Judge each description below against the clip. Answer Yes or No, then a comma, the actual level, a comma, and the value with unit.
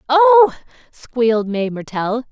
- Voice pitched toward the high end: Yes, very high, 265 Hz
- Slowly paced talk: Yes, slow, 105 wpm